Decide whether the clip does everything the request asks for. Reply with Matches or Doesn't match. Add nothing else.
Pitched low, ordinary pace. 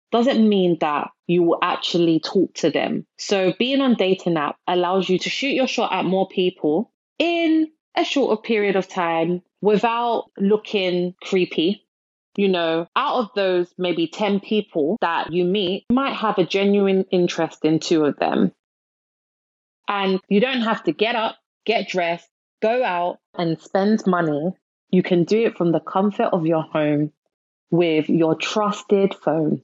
Doesn't match